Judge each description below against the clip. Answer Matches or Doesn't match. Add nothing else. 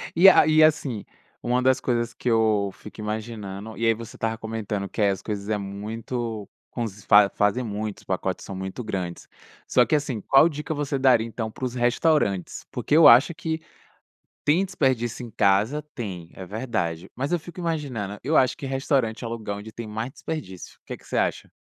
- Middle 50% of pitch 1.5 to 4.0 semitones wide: Doesn't match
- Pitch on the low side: Matches